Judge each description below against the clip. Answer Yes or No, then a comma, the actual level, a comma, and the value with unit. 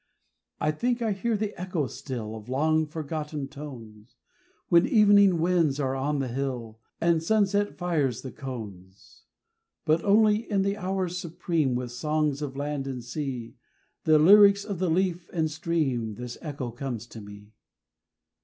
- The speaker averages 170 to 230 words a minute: No, average, 155 wpm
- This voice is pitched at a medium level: Yes, medium, 150 Hz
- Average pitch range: No, wide, 6.2 semitones